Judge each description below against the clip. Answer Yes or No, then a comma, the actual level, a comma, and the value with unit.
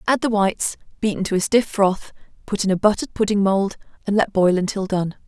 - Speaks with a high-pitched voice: Yes, high, 200 Hz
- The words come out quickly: Yes, fast, 215 wpm